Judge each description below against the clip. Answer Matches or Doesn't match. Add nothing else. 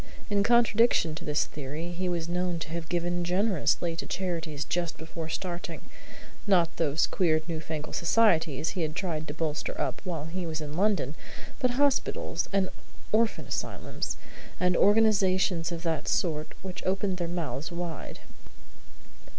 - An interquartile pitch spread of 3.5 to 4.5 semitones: Doesn't match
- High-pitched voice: Doesn't match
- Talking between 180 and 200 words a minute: Doesn't match